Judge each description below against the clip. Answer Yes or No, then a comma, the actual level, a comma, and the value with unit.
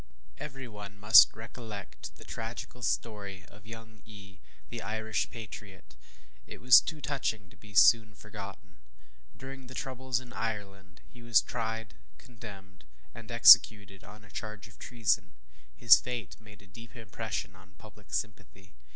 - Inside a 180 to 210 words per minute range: No, average, 145 wpm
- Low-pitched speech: Yes, low, 110 Hz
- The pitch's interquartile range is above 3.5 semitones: No, average, 2.8 semitones